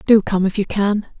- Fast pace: Yes, fast, 250 wpm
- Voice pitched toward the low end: No, high, 205 Hz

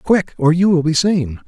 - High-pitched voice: No, medium, 165 Hz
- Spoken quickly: Yes, fast, 245 wpm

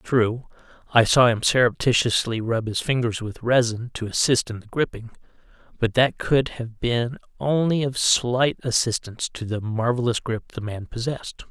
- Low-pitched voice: Yes, low, 120 Hz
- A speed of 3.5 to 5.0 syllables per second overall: Yes, 4.7 syllables/s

